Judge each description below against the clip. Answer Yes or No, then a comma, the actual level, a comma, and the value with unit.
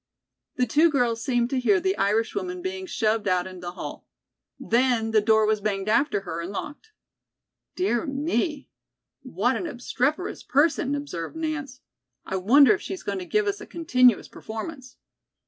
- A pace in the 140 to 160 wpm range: No, average, 170 wpm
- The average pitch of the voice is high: Yes, high, 245 Hz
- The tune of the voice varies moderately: No, wide, 6.0 semitones